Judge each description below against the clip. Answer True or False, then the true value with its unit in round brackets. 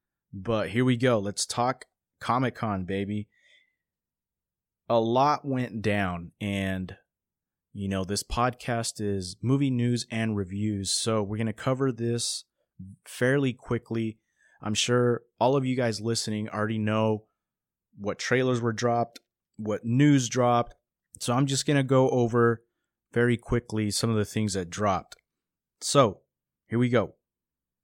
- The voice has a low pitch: True (115 Hz)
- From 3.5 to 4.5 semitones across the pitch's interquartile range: False (2.8 semitones)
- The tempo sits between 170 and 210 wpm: False (140 wpm)